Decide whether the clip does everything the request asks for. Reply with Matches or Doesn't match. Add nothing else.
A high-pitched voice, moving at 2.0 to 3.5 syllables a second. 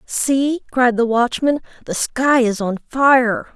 Matches